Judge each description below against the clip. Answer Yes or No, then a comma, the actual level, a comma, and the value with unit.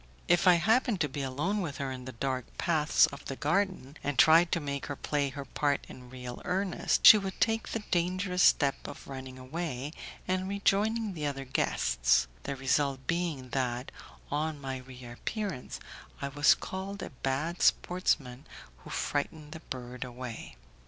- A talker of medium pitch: Yes, medium, 145 Hz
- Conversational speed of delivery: Yes, average, 165 wpm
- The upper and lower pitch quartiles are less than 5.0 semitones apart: No, wide, 5.4 semitones